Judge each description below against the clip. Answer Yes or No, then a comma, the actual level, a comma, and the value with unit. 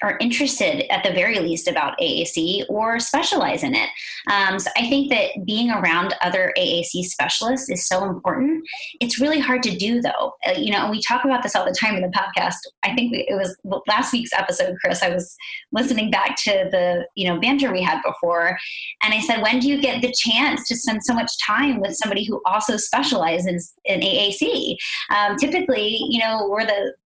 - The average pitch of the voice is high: Yes, high, 225 Hz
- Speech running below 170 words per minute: No, fast, 205 wpm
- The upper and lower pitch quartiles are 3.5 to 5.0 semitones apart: No, wide, 5.4 semitones